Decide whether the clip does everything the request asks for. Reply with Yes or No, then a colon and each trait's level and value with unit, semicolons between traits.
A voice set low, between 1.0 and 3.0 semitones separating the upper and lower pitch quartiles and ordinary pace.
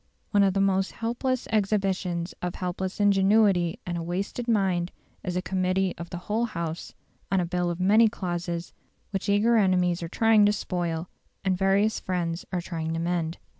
No: medium, 185 Hz; narrow, 2.6 semitones; average, 170 wpm